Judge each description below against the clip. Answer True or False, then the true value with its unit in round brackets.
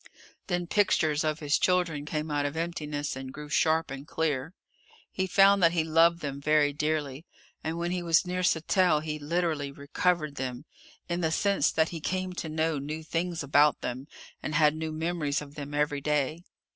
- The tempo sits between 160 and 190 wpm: True (185 wpm)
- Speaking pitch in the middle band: True (155 Hz)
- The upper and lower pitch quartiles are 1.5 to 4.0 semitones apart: True (2.6 semitones)